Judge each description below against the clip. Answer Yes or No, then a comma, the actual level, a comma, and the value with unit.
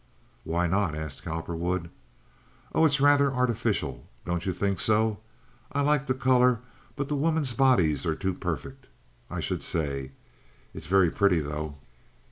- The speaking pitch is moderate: No, low, 100 Hz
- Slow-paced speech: No, average, 145 wpm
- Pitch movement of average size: No, wide, 8.3 semitones